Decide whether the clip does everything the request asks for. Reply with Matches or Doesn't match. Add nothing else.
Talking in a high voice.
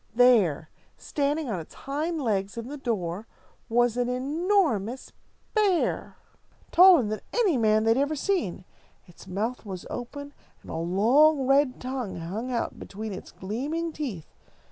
Matches